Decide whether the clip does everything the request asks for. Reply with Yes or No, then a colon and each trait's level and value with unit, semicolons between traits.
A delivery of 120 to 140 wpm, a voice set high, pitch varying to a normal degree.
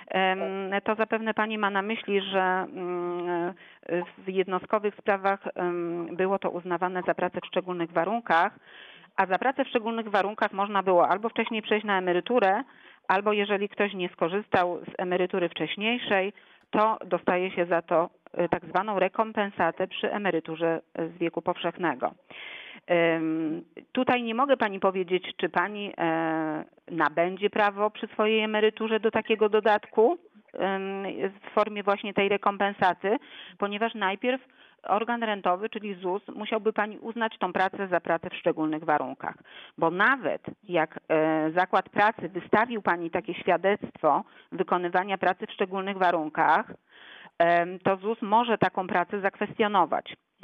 Yes: average, 130 wpm; high, 195 Hz; average, 3.4 semitones